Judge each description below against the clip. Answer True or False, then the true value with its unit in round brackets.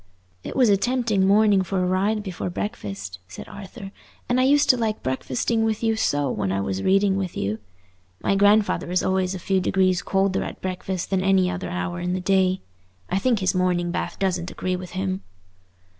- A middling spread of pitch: False (2.3 semitones)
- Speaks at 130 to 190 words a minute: False (205 wpm)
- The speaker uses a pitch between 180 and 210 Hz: True (190 Hz)